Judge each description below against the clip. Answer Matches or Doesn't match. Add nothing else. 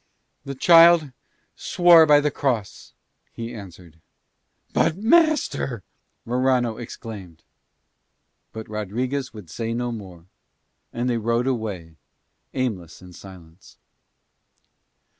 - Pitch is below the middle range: Matches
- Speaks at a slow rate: Matches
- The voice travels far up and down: Matches